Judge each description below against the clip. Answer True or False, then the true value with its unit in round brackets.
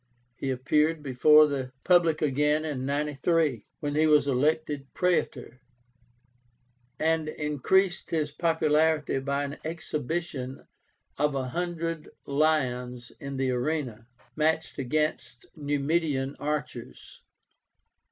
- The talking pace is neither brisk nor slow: False (105 wpm)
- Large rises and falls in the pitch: False (2.8 semitones)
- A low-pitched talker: False (150 Hz)